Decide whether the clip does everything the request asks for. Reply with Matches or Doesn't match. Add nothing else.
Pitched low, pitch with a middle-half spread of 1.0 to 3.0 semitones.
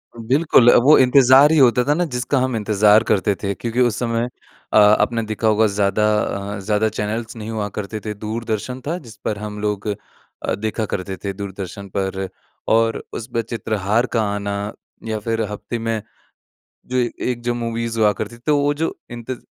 Matches